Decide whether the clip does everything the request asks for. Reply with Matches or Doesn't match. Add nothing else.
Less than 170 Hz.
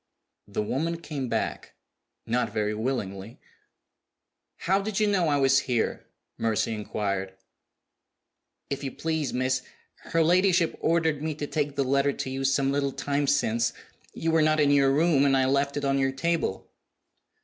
Matches